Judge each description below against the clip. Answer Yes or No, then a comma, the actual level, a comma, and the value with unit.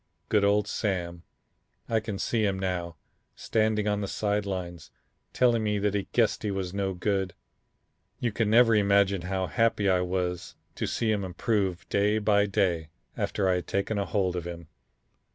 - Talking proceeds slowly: No, average, 175 wpm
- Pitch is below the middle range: Yes, low, 100 Hz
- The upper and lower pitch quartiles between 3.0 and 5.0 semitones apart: No, narrow, 2.5 semitones